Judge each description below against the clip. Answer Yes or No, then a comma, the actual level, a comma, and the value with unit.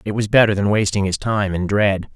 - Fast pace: Yes, fast, 250 wpm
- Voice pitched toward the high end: No, low, 100 Hz